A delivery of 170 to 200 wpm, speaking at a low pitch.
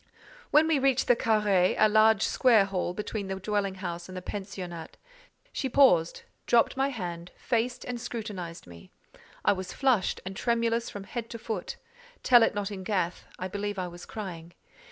No: average, 175 wpm; high, 205 Hz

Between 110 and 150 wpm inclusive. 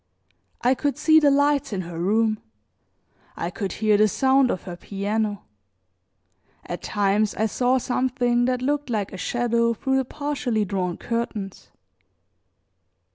Yes: average, 140 wpm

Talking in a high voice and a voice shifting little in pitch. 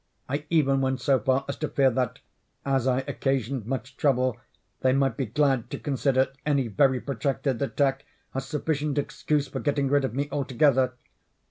No: low, 135 Hz; narrow, 1.5 semitones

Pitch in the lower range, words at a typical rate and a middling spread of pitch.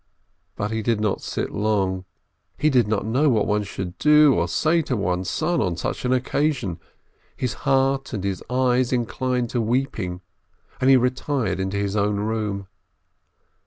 Yes: low, 115 Hz; average, 165 wpm; average, 4.7 semitones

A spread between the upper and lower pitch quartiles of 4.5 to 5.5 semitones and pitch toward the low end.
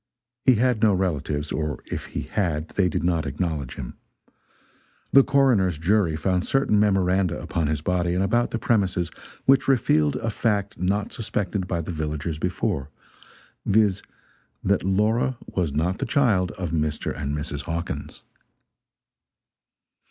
Yes: average, 5.1 semitones; very low, 90 Hz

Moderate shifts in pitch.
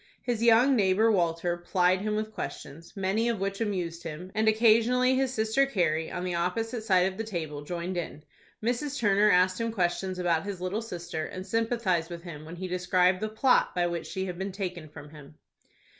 Yes: average, 4.1 semitones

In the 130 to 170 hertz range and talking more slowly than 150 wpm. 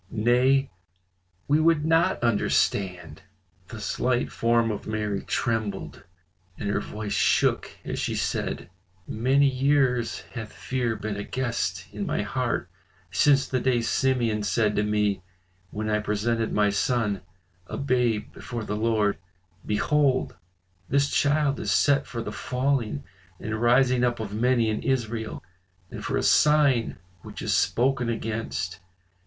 No: low, 115 Hz; average, 140 wpm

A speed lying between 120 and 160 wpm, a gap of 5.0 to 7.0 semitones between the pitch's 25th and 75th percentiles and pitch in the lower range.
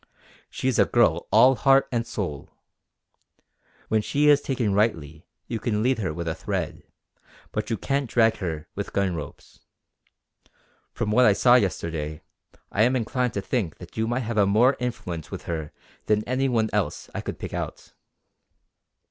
No: average, 170 wpm; wide, 5.4 semitones; low, 110 Hz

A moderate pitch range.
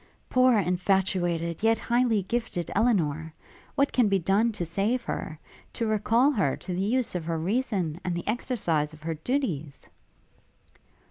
No: wide, 5.8 semitones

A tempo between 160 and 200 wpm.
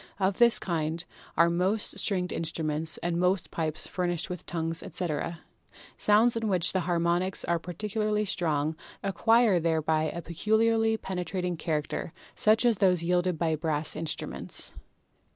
No: average, 145 wpm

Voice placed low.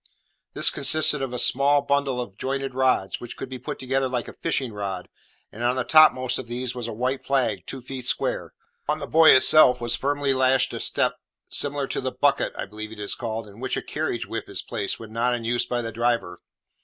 Yes: low, 125 Hz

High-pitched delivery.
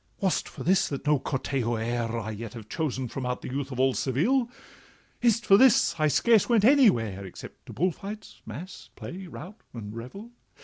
No: medium, 140 Hz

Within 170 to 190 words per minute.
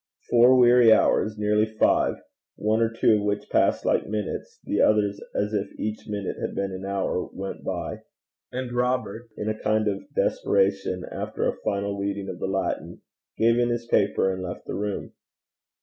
Yes: average, 180 wpm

